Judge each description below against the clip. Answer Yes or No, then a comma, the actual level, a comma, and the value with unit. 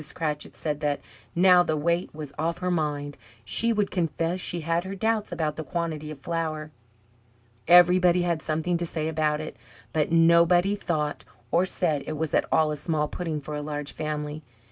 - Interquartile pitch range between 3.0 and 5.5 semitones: No, narrow, 2.5 semitones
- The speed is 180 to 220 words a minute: Yes, average, 185 wpm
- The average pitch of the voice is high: No, medium, 160 Hz